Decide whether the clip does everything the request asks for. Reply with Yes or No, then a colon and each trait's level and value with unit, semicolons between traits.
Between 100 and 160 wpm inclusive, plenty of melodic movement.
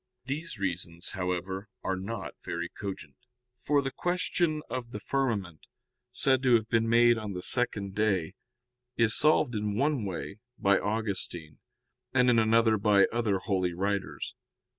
No: average, 145 wpm; average, 4.2 semitones